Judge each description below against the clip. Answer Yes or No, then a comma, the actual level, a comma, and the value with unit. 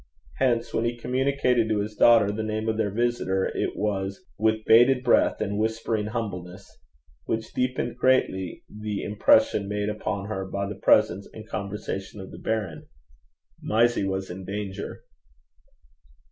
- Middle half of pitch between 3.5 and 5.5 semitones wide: No, narrow, 2.6 semitones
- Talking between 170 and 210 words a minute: No, average, 145 wpm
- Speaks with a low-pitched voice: Yes, low, 105 Hz